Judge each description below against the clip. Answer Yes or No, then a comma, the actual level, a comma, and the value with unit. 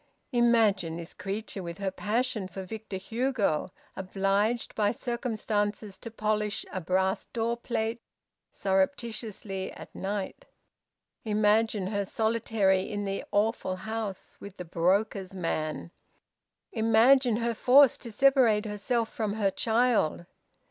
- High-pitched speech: Yes, high, 210 Hz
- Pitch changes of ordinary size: Yes, average, 3.0 semitones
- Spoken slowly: Yes, slow, 120 wpm